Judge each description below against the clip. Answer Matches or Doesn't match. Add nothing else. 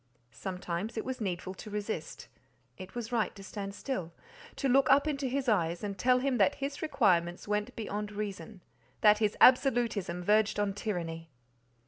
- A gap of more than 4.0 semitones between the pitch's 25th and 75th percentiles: Matches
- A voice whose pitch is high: Matches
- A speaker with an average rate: Matches